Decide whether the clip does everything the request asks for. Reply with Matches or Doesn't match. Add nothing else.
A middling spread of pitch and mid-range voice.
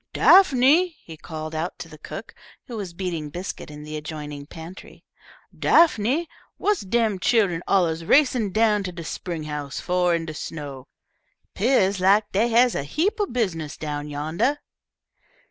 Doesn't match